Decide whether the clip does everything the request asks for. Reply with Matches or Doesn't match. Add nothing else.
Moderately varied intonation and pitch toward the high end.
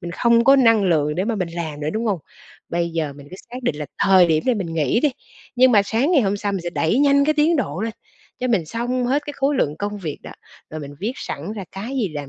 Doesn't match